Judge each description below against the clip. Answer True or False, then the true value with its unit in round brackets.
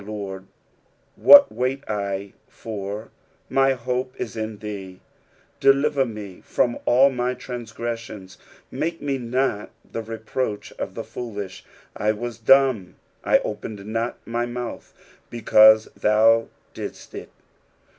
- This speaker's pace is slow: True (130 wpm)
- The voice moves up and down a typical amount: True (3.3 semitones)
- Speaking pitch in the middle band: False (115 Hz)